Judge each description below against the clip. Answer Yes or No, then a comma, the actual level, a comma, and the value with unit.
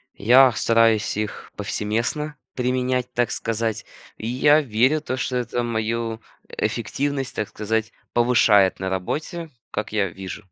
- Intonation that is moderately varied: Yes, average, 3.0 semitones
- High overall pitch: No, low, 115 Hz